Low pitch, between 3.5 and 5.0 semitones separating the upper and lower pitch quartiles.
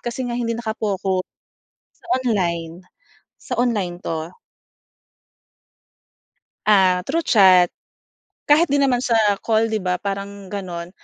No: high, 200 Hz; average, 4.6 semitones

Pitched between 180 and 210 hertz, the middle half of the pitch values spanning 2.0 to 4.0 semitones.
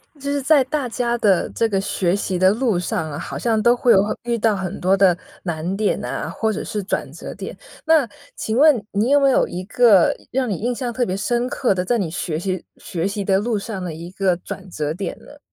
No: high, 205 Hz; average, 4.6 semitones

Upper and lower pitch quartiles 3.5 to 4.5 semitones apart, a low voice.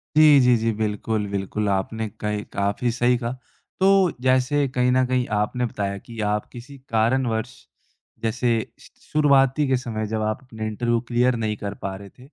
No: average, 3.1 semitones; low, 115 Hz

